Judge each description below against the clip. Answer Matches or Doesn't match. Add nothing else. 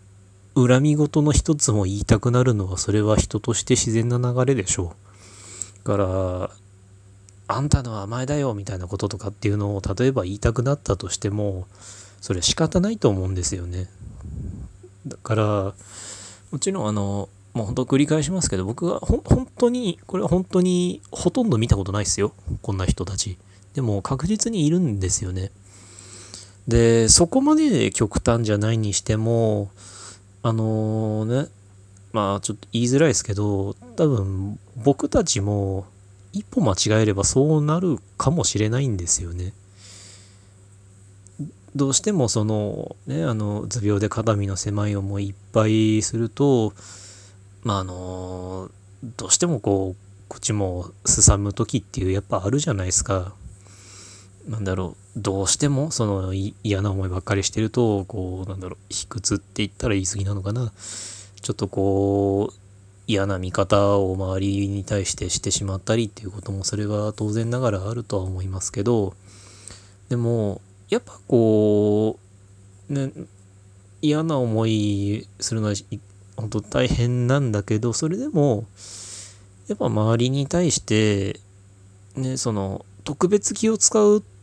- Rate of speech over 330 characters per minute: Doesn't match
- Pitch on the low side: Matches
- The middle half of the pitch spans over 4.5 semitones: Doesn't match